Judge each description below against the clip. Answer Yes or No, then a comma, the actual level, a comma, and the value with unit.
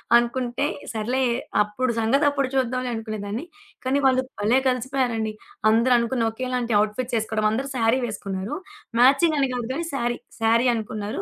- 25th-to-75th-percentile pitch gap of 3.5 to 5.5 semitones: No, average, 2.7 semitones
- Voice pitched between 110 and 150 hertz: No, high, 240 Hz